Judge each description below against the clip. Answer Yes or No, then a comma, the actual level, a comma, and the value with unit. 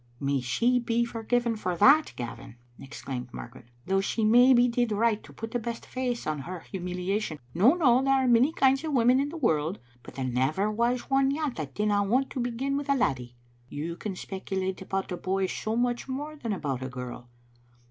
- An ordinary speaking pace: No, fast, 210 wpm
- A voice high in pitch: Yes, high, 215 Hz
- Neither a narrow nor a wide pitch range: No, wide, 6.8 semitones